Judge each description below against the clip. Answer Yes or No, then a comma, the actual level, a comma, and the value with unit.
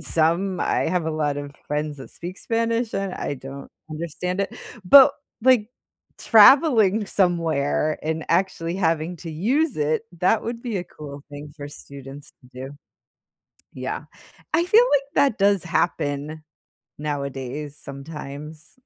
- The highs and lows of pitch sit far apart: Yes, wide, 5.8 semitones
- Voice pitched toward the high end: No, medium, 165 Hz